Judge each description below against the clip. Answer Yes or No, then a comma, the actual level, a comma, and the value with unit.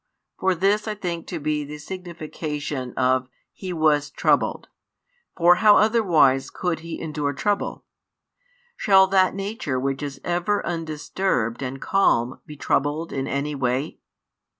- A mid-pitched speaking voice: Yes, medium, 155 Hz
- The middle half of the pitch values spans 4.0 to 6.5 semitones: Yes, average, 5.1 semitones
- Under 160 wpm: Yes, slow, 135 wpm